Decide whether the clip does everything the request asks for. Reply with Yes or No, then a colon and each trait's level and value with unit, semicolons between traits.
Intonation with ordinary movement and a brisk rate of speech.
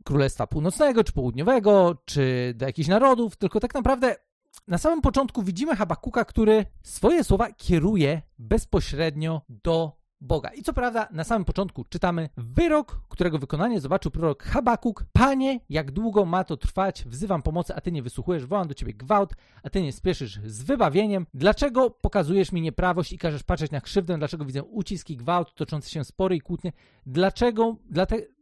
No: wide, 6.1 semitones; fast, 165 wpm